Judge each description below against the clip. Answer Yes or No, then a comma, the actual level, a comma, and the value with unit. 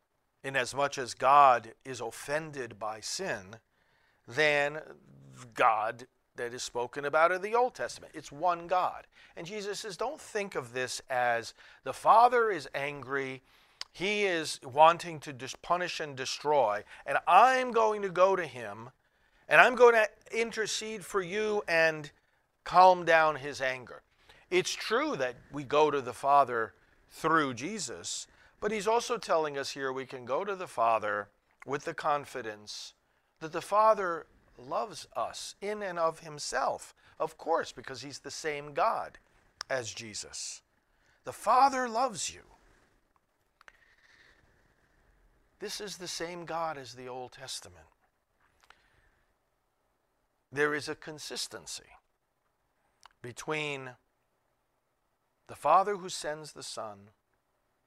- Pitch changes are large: Yes, wide, 6.4 semitones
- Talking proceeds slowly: Yes, slow, 130 wpm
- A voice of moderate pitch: Yes, medium, 155 Hz